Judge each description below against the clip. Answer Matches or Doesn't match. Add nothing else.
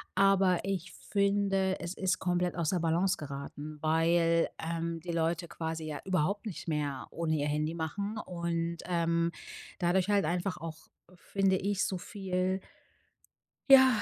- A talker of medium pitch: Matches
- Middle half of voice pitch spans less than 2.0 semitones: Doesn't match